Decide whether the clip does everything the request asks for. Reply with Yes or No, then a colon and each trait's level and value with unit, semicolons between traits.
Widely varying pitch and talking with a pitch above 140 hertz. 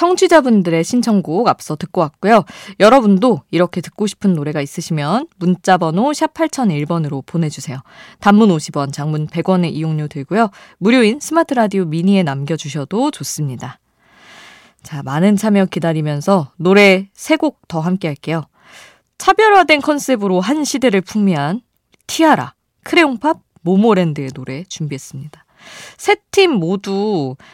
Yes: wide, 6.6 semitones; medium, 185 Hz